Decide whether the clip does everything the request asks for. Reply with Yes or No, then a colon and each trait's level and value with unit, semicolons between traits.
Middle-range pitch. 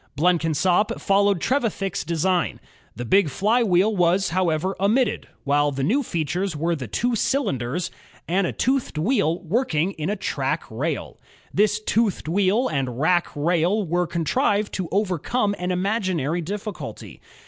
Yes: medium, 180 Hz